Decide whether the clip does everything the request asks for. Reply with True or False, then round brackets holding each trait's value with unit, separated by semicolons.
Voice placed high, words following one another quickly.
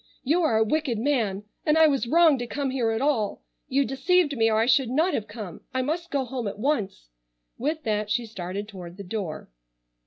True (245 Hz; 215 wpm)